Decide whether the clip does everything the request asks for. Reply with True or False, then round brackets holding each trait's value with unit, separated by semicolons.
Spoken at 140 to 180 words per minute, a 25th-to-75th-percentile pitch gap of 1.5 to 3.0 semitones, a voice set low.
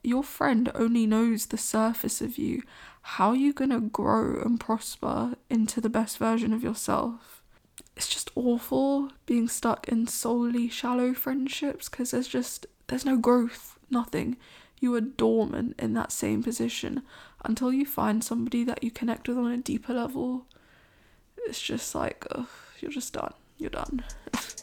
False (160 wpm; 2.5 semitones; 245 Hz)